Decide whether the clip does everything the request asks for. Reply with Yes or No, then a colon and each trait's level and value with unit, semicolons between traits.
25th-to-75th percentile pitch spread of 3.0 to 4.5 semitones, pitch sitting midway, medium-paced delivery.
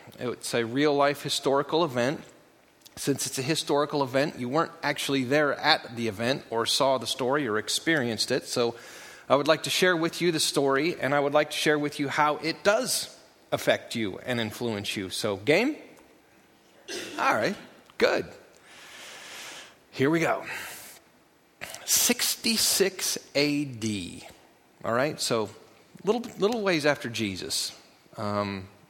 No: average, 5.2 semitones; medium, 145 Hz; average, 145 wpm